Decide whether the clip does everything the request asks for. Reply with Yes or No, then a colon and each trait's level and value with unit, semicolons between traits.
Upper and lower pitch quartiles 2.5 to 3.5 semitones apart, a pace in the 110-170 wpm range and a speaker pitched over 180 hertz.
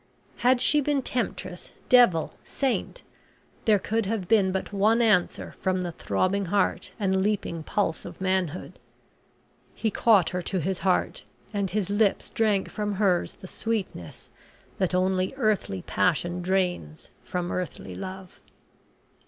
Yes: average, 2.9 semitones; slow, 135 wpm; high, 190 Hz